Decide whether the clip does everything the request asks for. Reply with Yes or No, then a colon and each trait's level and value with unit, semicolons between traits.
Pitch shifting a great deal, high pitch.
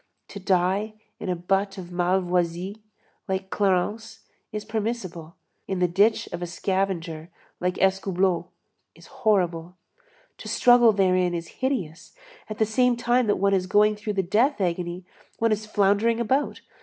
No: average, 3.3 semitones; high, 195 Hz